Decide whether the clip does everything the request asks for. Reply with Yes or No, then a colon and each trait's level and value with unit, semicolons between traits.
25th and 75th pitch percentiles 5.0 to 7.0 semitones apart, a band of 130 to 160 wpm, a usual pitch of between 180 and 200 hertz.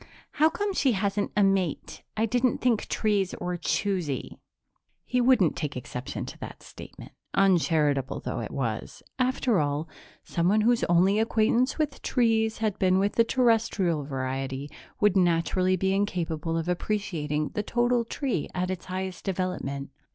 Yes: wide, 5.4 semitones; average, 150 wpm; high, 190 Hz